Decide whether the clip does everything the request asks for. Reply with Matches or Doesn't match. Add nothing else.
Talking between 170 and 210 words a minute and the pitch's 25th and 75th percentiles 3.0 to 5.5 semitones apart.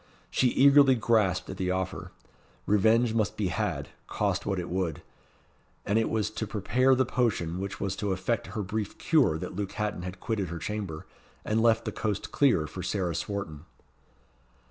Matches